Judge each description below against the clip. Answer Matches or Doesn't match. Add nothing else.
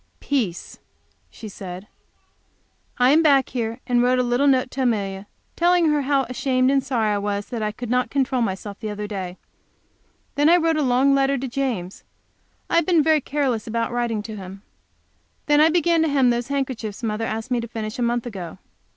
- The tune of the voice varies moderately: Matches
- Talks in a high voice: Matches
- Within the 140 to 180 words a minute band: Doesn't match